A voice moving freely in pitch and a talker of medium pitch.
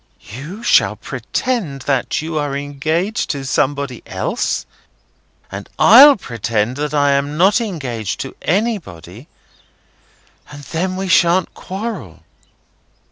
Yes: wide, 5.9 semitones; medium, 150 Hz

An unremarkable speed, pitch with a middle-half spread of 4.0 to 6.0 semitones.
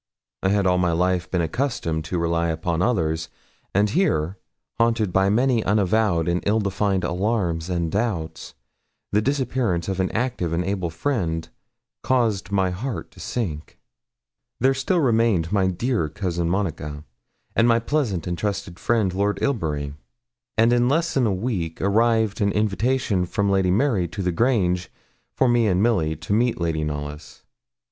Yes: average, 160 wpm; average, 5.1 semitones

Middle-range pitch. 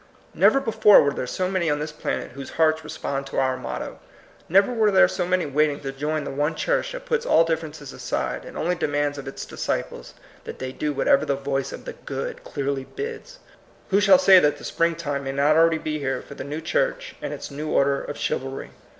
Yes: medium, 155 Hz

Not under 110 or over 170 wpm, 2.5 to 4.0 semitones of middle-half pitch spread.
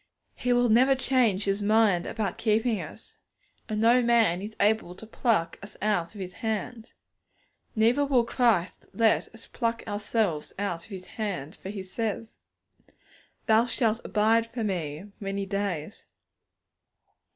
Yes: average, 145 wpm; average, 2.8 semitones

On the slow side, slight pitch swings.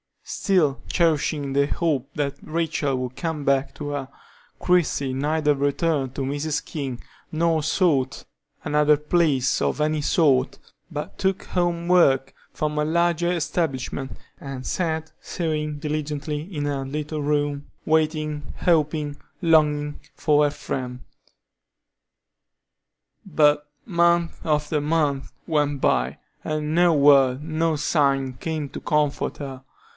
Yes: slow, 120 wpm; narrow, 2.2 semitones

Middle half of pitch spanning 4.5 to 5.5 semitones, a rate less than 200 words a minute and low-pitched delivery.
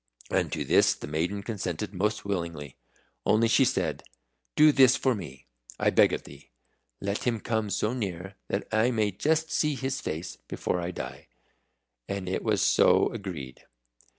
Yes: average, 5.2 semitones; average, 165 wpm; low, 100 Hz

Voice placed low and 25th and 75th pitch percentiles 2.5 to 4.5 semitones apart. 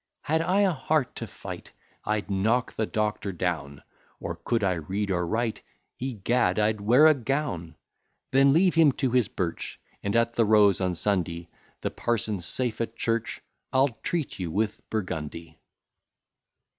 No: low, 110 Hz; average, 5.3 semitones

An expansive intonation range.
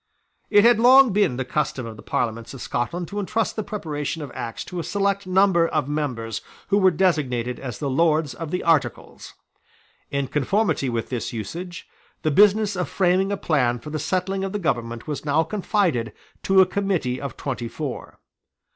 Yes: wide, 7.0 semitones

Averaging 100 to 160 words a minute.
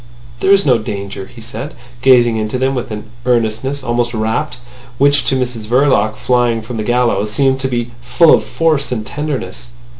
No: average, 180 wpm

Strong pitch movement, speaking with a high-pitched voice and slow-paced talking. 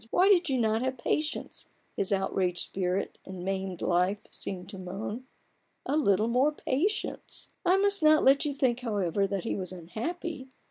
No: wide, 7.6 semitones; high, 225 Hz; average, 170 wpm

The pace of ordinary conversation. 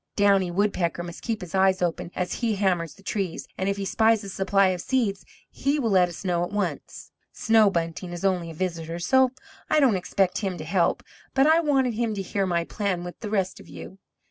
No: fast, 220 wpm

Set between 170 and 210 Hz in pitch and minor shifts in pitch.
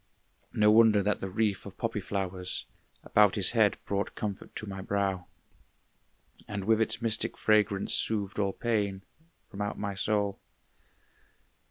No: low, 100 Hz; narrow, 1.7 semitones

